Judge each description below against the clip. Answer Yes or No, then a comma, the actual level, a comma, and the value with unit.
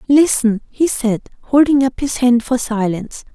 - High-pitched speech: Yes, high, 245 Hz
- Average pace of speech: Yes, average, 160 wpm